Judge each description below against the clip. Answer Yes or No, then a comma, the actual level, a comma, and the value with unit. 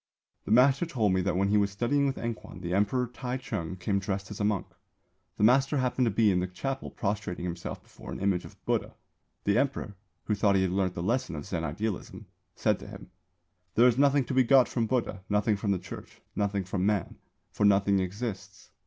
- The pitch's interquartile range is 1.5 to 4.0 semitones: No, average, 4.4 semitones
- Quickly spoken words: Yes, fast, 215 wpm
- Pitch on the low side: Yes, low, 105 Hz